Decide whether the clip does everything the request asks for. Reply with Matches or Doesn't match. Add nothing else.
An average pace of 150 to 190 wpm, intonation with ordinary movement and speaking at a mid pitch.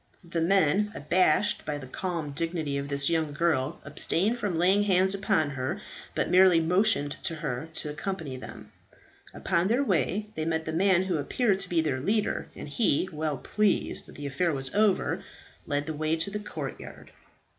Matches